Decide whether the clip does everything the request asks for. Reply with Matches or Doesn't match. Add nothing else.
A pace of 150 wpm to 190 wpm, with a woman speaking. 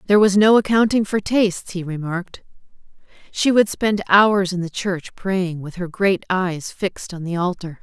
Matches